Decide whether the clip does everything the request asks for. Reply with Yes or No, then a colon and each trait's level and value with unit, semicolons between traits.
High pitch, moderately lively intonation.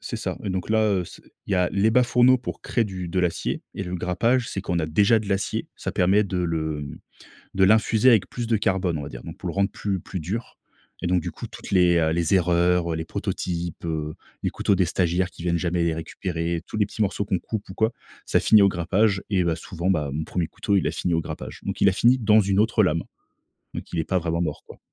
No: very low, 90 Hz; average, 3.2 semitones